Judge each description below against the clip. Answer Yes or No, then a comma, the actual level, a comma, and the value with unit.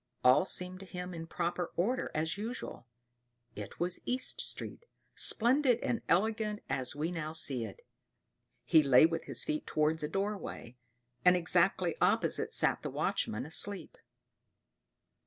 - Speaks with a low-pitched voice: No, medium, 175 Hz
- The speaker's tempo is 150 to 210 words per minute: No, average, 140 wpm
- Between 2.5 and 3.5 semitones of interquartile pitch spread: No, average, 4.6 semitones